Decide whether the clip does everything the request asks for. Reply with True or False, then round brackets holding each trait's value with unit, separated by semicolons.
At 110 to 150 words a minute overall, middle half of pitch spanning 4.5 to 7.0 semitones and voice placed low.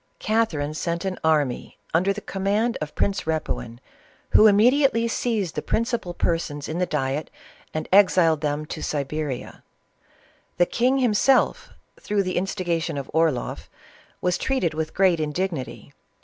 False (140 wpm; 5.1 semitones; 175 Hz)